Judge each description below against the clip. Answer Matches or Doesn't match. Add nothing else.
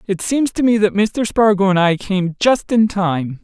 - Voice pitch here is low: Doesn't match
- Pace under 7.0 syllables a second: Matches